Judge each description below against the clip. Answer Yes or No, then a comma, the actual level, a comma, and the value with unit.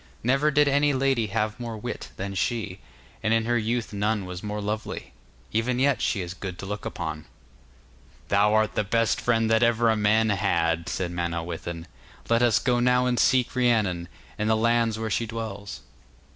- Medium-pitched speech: No, low, 110 Hz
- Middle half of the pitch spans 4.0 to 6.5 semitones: No, average, 3.2 semitones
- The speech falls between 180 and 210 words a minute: Yes, average, 185 wpm